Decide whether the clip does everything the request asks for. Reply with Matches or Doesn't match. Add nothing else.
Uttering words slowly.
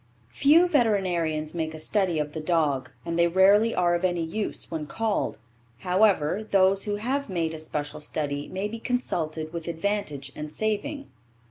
Doesn't match